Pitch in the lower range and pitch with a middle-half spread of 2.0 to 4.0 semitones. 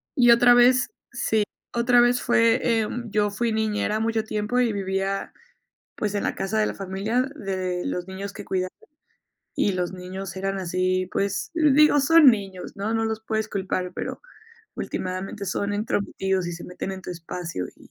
No: high, 205 Hz; average, 3.3 semitones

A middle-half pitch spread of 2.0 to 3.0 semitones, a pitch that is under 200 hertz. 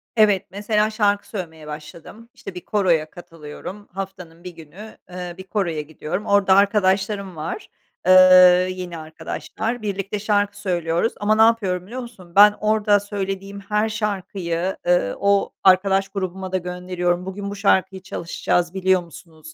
Yes: narrow, 2.6 semitones; high, 190 Hz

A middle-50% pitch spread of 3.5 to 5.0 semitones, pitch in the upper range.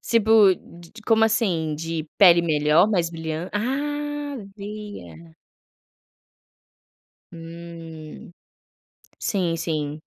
No: average, 4.4 semitones; medium, 170 Hz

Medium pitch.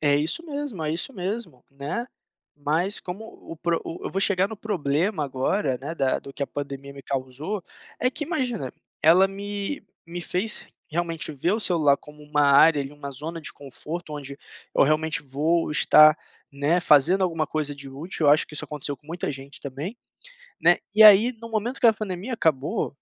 Yes: medium, 160 Hz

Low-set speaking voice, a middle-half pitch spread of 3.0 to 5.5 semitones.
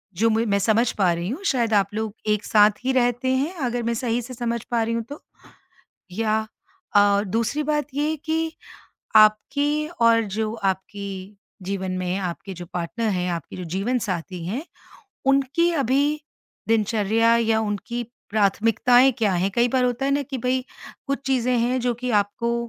No: high, 230 Hz; average, 3.8 semitones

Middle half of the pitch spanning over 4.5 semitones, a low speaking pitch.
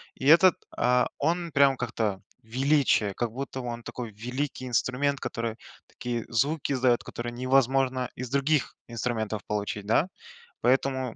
No: average, 2.8 semitones; low, 125 Hz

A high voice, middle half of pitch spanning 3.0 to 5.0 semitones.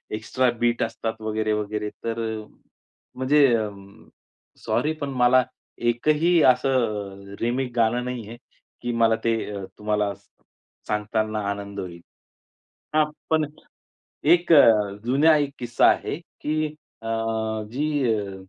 No: low, 115 Hz; average, 3.6 semitones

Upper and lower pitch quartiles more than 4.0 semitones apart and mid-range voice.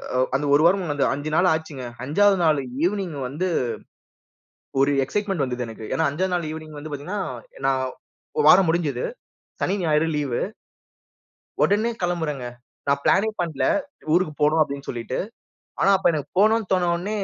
Yes: average, 4.6 semitones; medium, 155 Hz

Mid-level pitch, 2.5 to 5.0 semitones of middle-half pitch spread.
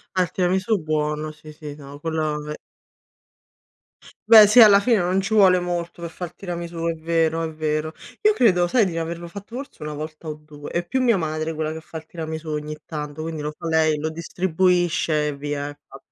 Yes: medium, 160 Hz; average, 2.8 semitones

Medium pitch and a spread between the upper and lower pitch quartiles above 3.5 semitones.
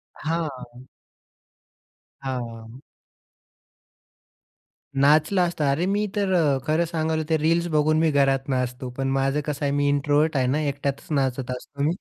No: medium, 145 Hz; average, 2.9 semitones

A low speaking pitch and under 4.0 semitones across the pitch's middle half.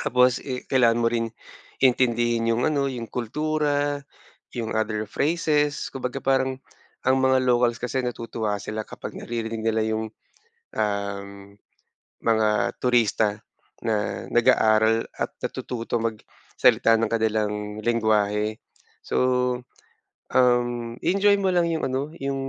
Yes: low, 120 Hz; average, 3.1 semitones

